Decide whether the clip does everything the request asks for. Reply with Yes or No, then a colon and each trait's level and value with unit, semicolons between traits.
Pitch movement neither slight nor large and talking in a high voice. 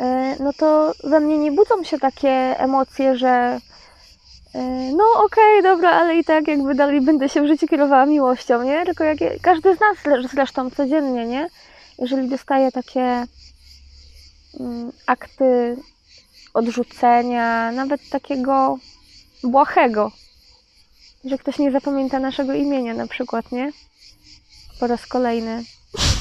Yes: average, 3.2 semitones; very high, 270 Hz